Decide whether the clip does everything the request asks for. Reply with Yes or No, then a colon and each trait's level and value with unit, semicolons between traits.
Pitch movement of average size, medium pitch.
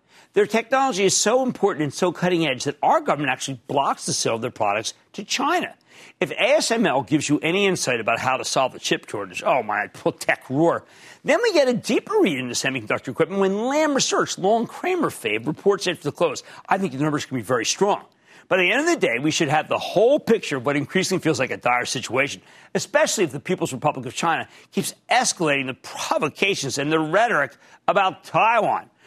No: wide, 8.2 semitones; medium, 175 Hz